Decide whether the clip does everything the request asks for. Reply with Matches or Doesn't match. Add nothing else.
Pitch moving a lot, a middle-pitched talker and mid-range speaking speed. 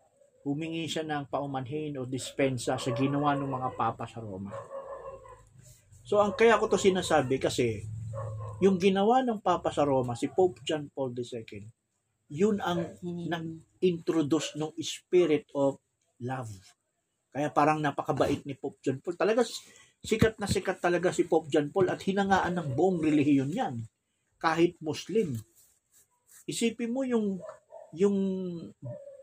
Matches